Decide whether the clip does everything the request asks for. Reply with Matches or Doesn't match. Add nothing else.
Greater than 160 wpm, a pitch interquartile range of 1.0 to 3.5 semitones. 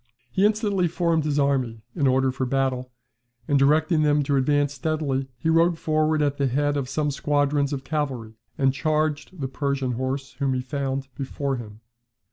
Matches